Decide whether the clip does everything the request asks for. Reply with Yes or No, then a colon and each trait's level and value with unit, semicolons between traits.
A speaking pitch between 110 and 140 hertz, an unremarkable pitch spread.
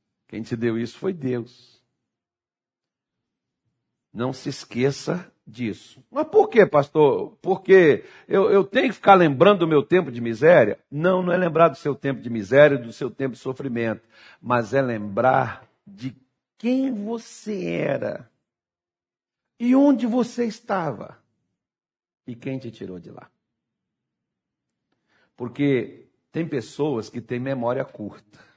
No: low, 135 Hz; wide, 8.7 semitones